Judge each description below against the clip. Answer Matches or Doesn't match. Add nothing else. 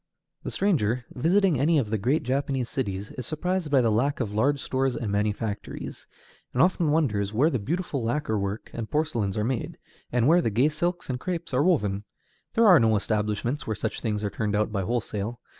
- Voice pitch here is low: Matches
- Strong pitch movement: Matches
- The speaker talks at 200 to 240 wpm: Matches